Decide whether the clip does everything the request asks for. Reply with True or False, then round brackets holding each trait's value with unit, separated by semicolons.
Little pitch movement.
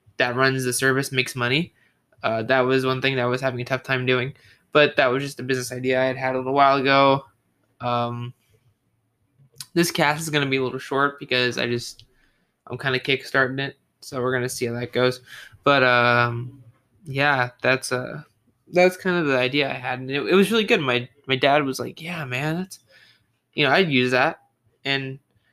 True (2.2 semitones)